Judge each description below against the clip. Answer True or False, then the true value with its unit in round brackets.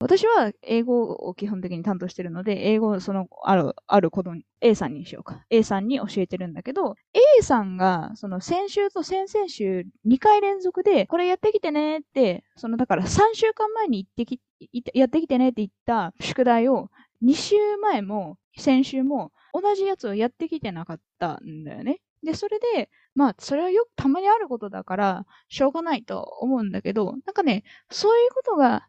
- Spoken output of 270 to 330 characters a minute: False (355 characters per minute)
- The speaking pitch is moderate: False (255 Hz)